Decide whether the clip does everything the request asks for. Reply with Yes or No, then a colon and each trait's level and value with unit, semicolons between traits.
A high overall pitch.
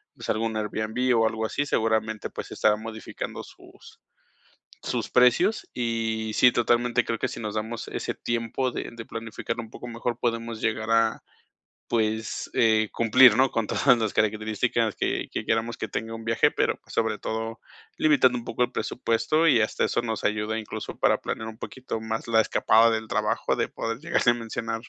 No: low, 115 Hz